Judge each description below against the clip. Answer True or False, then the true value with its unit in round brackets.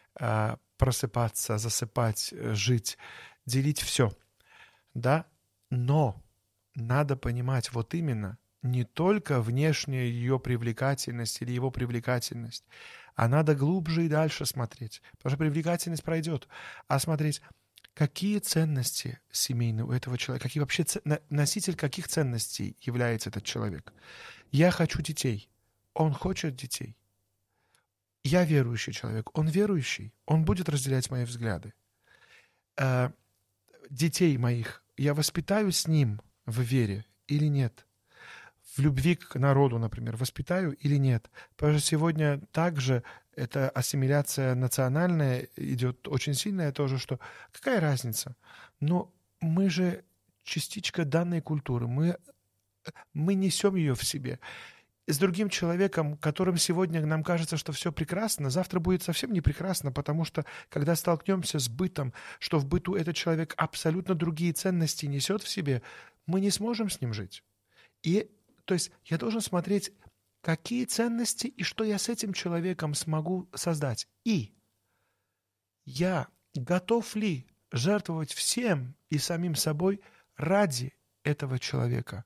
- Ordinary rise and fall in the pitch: False (5.8 semitones)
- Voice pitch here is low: False (145 Hz)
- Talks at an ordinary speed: True (125 wpm)